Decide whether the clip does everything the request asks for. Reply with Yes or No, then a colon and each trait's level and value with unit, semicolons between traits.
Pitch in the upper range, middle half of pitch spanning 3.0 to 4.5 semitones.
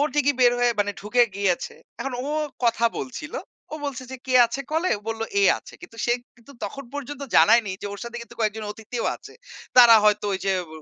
Yes: high, 235 Hz; average, 3.8 semitones